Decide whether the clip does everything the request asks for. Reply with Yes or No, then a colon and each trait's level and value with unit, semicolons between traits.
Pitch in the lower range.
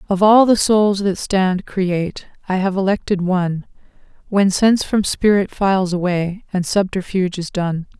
No: high, 190 Hz